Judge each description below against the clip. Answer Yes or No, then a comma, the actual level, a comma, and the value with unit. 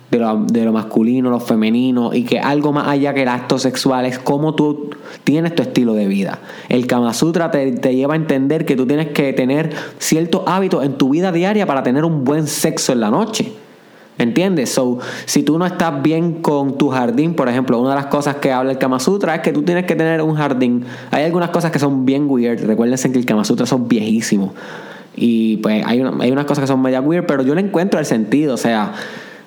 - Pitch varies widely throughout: No, average, 4.0 semitones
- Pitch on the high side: No, medium, 140 Hz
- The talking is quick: Yes, fast, 230 wpm